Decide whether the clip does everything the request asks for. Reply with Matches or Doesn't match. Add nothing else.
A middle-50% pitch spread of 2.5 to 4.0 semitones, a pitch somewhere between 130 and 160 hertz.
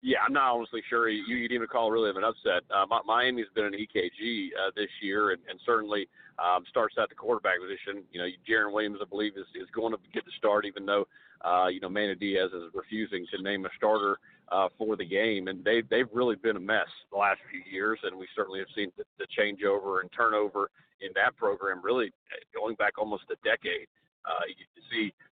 Doesn't match